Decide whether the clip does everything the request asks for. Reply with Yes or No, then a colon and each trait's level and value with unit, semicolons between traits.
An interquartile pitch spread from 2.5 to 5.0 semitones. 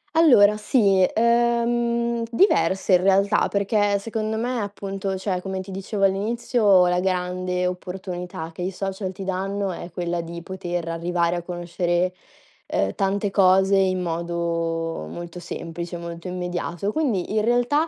Yes: average, 2.8 semitones